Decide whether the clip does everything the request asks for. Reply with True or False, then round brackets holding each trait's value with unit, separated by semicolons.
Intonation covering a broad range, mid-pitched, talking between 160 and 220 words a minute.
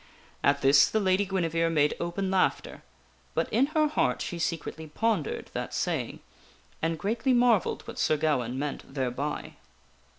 False (6.4 semitones; 165 Hz; 145 wpm)